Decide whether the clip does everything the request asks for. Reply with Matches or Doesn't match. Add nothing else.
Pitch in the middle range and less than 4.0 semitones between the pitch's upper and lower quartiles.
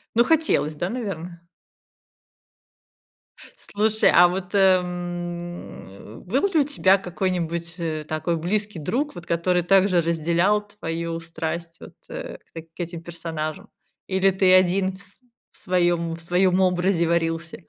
Matches